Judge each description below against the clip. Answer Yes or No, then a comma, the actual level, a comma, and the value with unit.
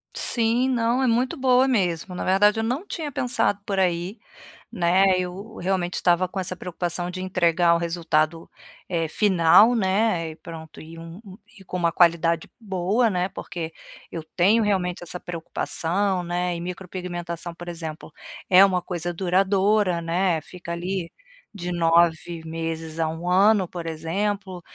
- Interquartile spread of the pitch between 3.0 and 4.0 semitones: No, narrow, 2.6 semitones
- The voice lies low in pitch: No, medium, 180 Hz